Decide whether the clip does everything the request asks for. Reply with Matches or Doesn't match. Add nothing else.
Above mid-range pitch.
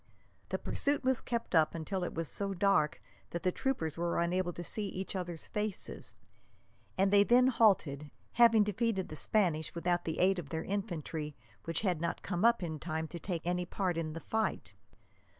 Doesn't match